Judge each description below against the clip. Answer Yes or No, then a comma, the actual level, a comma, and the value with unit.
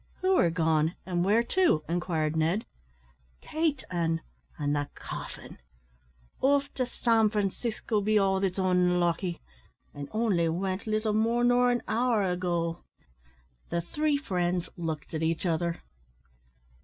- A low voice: No, medium, 185 Hz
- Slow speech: Yes, slow, 130 wpm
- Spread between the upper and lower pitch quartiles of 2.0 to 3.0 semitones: No, average, 5.2 semitones